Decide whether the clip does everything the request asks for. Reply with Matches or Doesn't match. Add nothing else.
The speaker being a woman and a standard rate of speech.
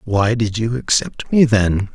Doesn't match